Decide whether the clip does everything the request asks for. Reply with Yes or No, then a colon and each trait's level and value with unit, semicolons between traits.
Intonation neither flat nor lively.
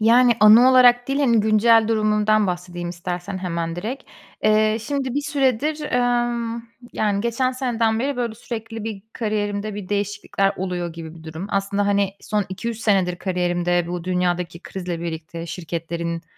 Yes: average, 4.7 semitones